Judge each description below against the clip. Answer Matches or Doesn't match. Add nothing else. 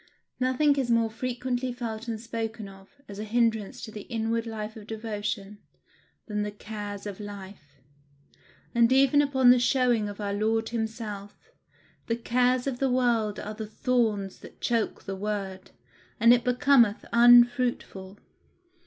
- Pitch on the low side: Doesn't match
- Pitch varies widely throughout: Doesn't match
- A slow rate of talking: Doesn't match